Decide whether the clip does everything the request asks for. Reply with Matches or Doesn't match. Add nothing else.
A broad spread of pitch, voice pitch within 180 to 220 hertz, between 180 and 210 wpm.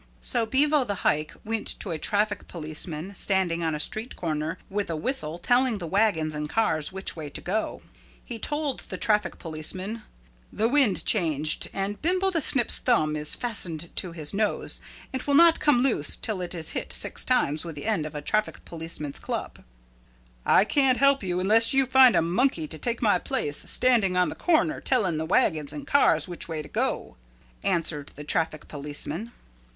Matches